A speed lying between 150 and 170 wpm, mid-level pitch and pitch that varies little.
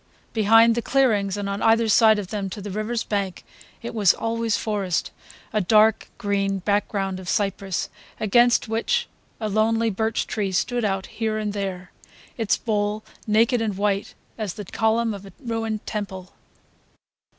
No: average, 160 wpm; high, 210 Hz; narrow, 2.2 semitones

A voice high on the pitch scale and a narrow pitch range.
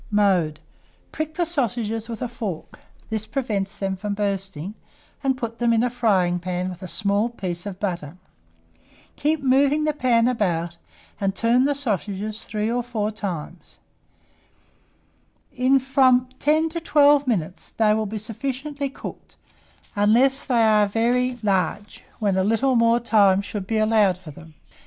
No: high, 220 Hz; average, 4.5 semitones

